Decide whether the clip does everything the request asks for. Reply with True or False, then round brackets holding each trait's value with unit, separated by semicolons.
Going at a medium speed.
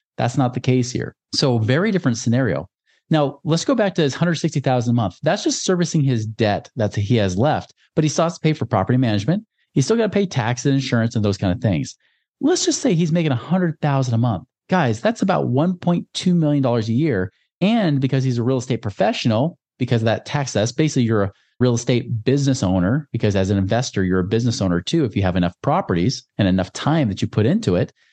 False (225 wpm)